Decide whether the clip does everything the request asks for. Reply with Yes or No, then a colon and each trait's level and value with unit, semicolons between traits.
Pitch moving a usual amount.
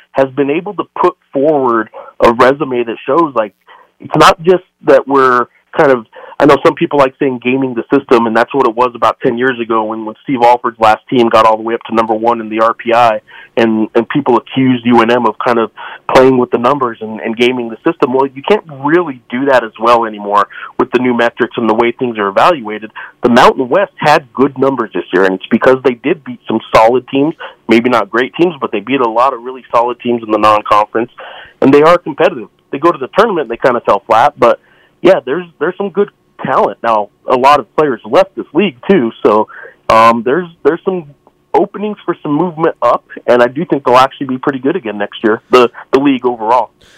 Yes: average, 3.8 semitones